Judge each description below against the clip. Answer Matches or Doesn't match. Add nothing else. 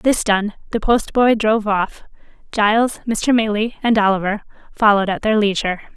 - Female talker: Matches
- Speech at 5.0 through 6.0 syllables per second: Matches